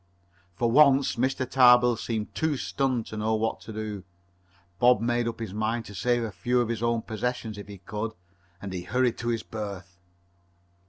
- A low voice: Yes, low, 115 Hz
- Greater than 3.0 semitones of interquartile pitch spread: No, narrow, 2.4 semitones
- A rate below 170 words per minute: No, average, 190 wpm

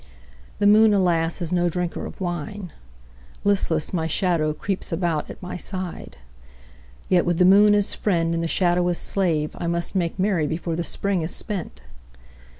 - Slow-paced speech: No, average, 170 wpm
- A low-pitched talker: No, medium, 175 Hz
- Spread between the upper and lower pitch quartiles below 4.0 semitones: Yes, narrow, 2.5 semitones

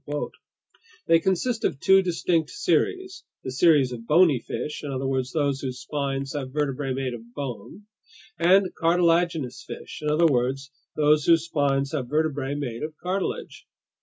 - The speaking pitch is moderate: Yes, medium, 145 Hz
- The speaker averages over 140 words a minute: Yes, average, 155 wpm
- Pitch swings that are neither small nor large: Yes, average, 4.0 semitones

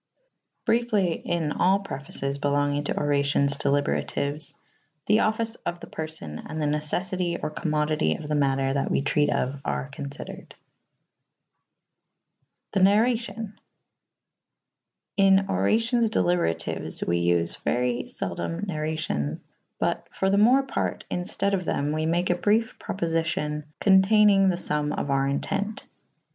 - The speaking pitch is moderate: Yes, medium, 155 Hz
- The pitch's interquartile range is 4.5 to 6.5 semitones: Yes, wide, 5.5 semitones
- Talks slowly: Yes, slow, 130 wpm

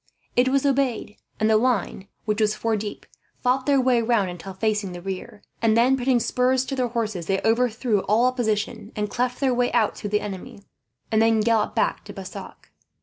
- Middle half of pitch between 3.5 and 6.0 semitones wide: No, average, 3.1 semitones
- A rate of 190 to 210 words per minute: Yes, average, 200 wpm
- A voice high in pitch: Yes, high, 225 Hz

